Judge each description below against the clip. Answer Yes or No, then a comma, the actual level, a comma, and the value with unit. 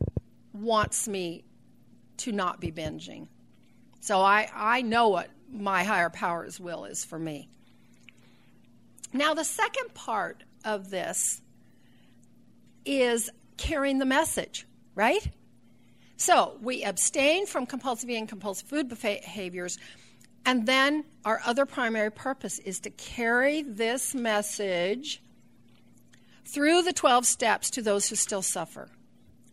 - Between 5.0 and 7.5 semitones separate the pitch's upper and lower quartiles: Yes, average, 5.3 semitones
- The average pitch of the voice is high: Yes, high, 230 Hz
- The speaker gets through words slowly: Yes, slow, 120 wpm